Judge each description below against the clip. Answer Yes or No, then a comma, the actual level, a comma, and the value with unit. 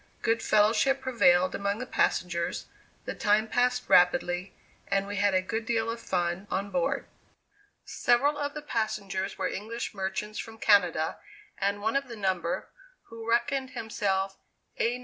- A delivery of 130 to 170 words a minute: Yes, average, 155 wpm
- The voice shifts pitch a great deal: No, average, 3.7 semitones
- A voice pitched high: Yes, high, 210 Hz